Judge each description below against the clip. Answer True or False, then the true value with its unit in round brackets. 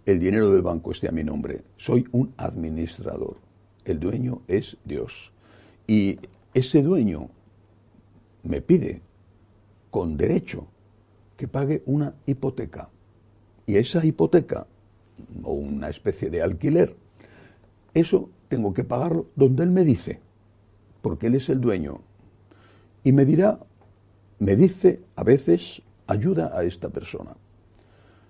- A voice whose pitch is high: False (105 Hz)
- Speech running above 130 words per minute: False (125 wpm)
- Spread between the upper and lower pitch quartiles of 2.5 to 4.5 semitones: True (4.2 semitones)